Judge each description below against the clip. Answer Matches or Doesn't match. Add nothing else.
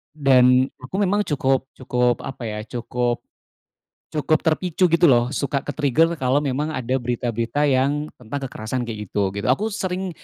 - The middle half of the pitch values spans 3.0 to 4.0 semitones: Matches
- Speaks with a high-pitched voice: Doesn't match